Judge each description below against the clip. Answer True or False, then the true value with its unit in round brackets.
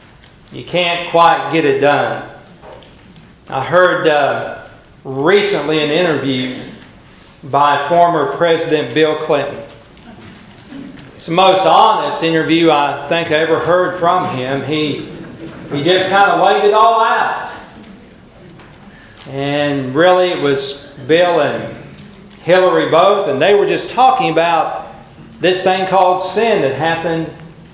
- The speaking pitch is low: False (165 Hz)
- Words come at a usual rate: False (125 wpm)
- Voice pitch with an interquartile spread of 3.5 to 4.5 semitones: True (4.1 semitones)